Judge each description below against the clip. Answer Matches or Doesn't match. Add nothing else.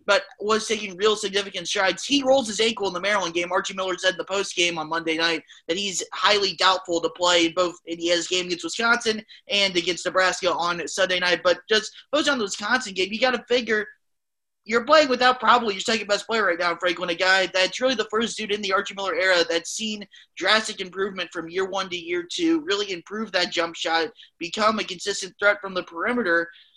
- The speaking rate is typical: Doesn't match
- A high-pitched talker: Matches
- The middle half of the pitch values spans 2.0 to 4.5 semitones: Matches